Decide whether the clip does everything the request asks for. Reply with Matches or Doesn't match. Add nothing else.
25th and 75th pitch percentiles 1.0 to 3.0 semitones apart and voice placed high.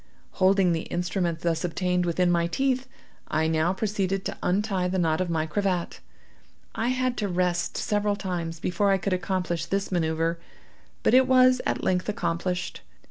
Doesn't match